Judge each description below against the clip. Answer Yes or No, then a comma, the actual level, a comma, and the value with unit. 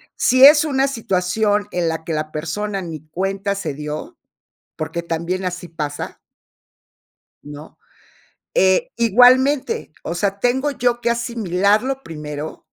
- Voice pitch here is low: No, high, 195 Hz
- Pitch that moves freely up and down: Yes, wide, 6.6 semitones